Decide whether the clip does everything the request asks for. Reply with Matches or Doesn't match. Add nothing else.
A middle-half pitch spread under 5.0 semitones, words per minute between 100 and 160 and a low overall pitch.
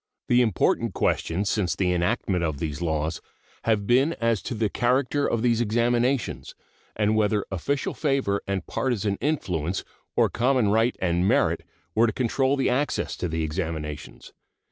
Doesn't match